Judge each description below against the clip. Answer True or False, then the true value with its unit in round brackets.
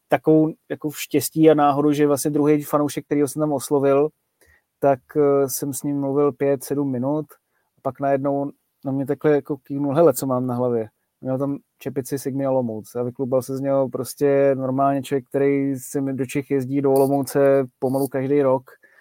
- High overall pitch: False (140 Hz)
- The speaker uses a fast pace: True (185 wpm)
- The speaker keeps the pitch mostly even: True (1.2 semitones)